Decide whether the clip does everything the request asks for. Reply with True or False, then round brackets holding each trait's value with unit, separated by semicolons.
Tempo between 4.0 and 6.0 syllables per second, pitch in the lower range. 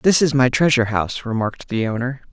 False (6.4 syllables/s; 130 Hz)